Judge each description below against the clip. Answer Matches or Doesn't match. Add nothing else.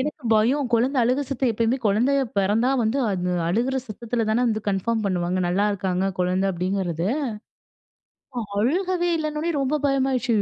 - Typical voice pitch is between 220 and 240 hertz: Matches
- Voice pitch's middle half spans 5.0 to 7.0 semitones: Matches